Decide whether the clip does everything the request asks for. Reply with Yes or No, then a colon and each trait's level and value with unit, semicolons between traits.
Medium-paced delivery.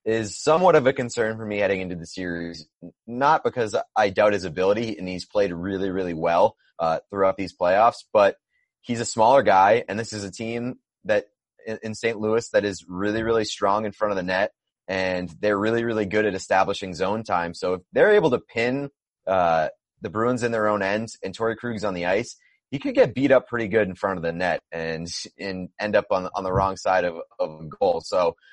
No: fast, 220 wpm